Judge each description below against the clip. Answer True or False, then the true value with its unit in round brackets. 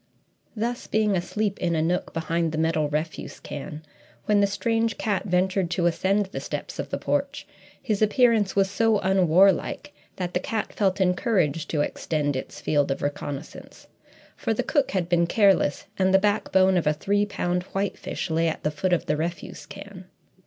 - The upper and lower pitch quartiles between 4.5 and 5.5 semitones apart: False (3.7 semitones)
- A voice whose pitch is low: False (185 Hz)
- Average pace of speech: True (180 wpm)